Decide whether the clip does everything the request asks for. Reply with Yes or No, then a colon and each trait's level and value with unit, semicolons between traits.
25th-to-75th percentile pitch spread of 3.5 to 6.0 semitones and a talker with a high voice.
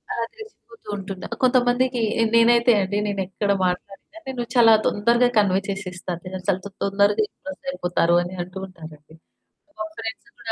Yes: average, 4.4 semitones; high, 200 Hz